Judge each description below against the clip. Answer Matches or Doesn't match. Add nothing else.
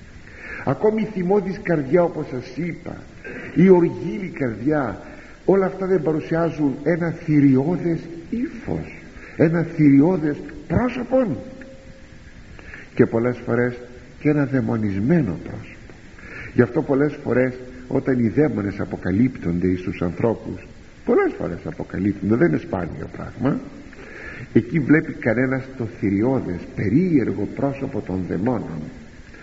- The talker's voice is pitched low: Matches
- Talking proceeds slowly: Matches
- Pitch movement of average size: Doesn't match